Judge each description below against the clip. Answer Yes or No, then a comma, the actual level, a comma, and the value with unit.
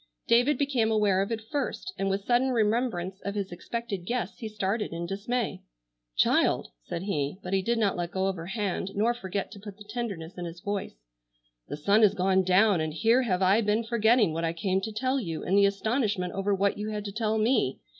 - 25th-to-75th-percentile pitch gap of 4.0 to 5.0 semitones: No, average, 3.3 semitones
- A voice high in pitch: Yes, high, 205 Hz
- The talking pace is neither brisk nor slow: No, fast, 215 wpm